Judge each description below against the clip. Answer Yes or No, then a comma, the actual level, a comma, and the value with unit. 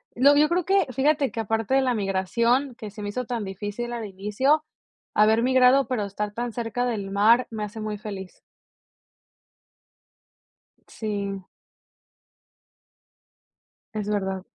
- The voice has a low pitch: No, high, 225 Hz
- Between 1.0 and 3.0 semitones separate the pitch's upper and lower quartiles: No, average, 3.6 semitones